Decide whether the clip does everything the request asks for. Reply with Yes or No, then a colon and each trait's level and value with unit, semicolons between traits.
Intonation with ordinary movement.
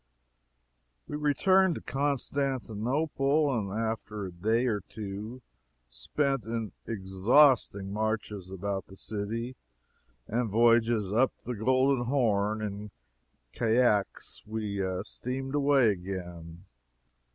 Yes: average, 4.4 semitones